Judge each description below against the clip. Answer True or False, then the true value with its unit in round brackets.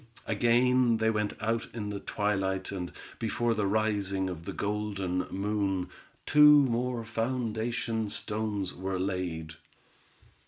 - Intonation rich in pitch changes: False (3.1 semitones)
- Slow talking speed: True (120 wpm)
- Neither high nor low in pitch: False (105 Hz)